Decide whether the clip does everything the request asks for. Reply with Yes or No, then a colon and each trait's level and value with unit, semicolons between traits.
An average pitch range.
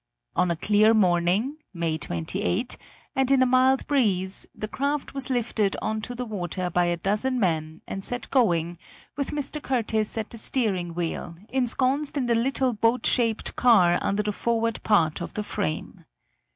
No: wide, 6.2 semitones